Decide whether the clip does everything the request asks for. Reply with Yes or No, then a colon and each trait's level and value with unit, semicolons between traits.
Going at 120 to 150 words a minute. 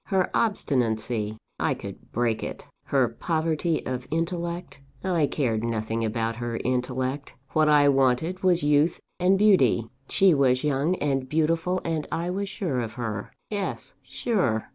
Yes: average, 145 wpm